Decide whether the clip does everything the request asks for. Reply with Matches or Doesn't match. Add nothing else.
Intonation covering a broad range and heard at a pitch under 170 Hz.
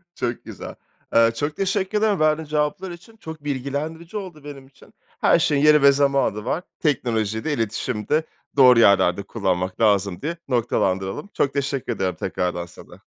Matches